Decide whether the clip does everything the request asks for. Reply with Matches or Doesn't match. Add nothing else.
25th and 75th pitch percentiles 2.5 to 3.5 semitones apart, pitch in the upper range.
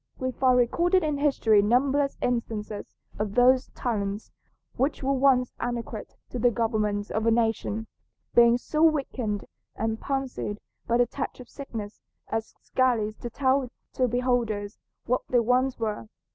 Matches